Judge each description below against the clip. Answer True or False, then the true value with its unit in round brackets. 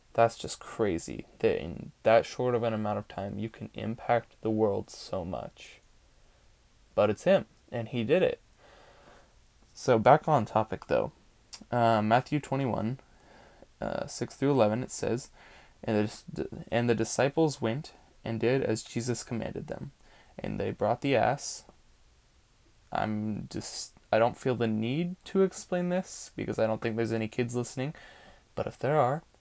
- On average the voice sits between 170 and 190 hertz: False (115 Hz)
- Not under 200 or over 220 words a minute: False (160 wpm)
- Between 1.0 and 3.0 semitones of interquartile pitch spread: False (3.9 semitones)